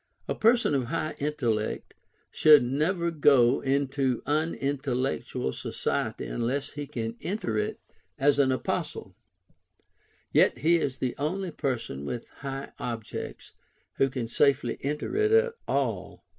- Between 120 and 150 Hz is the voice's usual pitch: Yes, medium, 140 Hz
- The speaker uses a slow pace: Yes, slow, 130 wpm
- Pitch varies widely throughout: No, average, 3.8 semitones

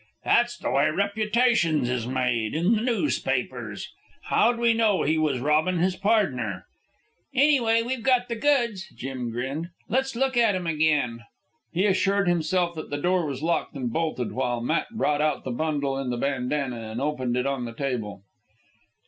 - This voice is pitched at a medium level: Yes, medium, 155 Hz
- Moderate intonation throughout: No, wide, 8.9 semitones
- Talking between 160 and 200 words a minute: Yes, average, 170 wpm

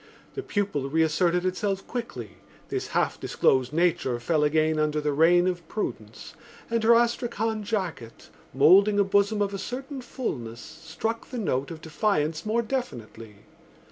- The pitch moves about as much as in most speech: No, wide, 6.2 semitones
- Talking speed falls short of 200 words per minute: Yes, average, 145 wpm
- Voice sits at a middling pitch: Yes, medium, 180 Hz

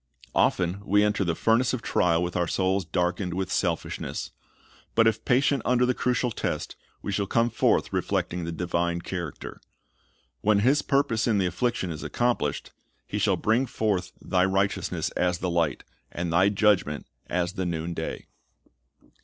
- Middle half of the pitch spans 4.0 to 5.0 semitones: Yes, average, 4.3 semitones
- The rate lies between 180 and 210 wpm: No, average, 160 wpm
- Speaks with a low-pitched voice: Yes, very low, 95 Hz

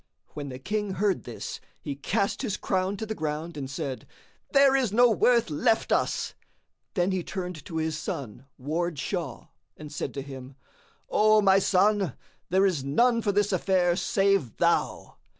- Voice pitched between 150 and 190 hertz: Yes, medium, 185 Hz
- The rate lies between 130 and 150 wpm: No, average, 170 wpm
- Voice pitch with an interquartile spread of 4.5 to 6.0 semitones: Yes, wide, 5.6 semitones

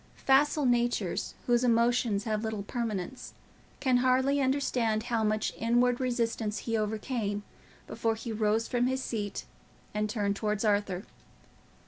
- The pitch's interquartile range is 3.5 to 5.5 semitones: No, average, 2.7 semitones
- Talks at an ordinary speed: No, slow, 130 wpm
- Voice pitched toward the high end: Yes, high, 230 Hz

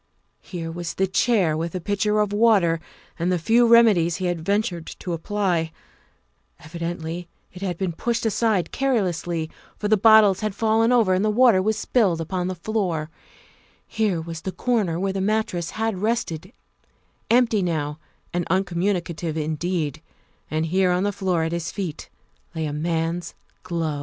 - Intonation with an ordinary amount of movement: Yes, average, 4.2 semitones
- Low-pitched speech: No, medium, 185 Hz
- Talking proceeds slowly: No, average, 165 wpm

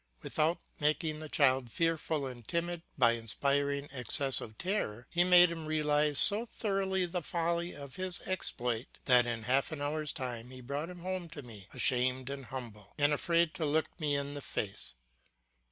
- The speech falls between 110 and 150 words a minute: No, average, 170 wpm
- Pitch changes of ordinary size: Yes, average, 4.9 semitones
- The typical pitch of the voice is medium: Yes, medium, 145 Hz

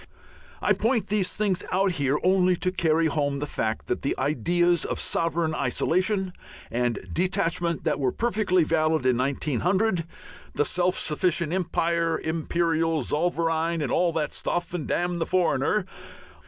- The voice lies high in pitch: No, medium, 170 Hz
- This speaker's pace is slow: No, average, 145 wpm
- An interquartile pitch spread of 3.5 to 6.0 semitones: No, average, 2.8 semitones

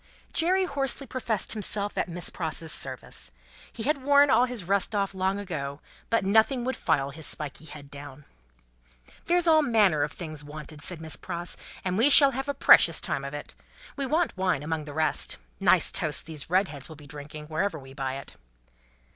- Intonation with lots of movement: Yes, wide, 8.2 semitones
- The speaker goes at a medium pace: Yes, average, 190 wpm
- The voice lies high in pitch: No, medium, 175 Hz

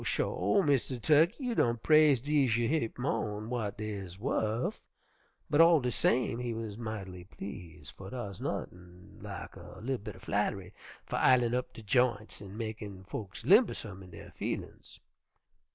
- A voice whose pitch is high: No, low, 110 Hz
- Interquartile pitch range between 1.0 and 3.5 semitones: No, average, 4.4 semitones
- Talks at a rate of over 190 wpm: No, average, 165 wpm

